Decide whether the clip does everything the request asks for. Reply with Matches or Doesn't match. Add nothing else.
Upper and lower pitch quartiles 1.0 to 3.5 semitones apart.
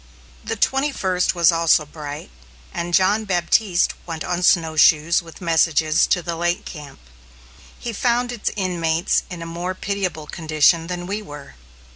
Matches